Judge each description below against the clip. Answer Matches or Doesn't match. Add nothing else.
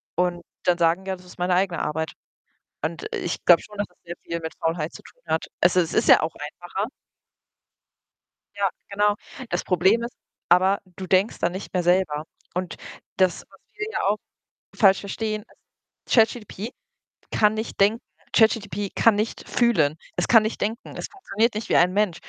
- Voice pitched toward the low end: Doesn't match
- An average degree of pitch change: Matches